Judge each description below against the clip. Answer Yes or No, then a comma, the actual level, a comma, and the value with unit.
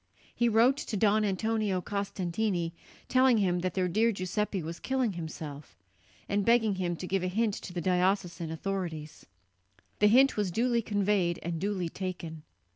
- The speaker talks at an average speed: Yes, average, 160 wpm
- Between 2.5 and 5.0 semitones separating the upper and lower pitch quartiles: Yes, average, 3.7 semitones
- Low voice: No, high, 195 Hz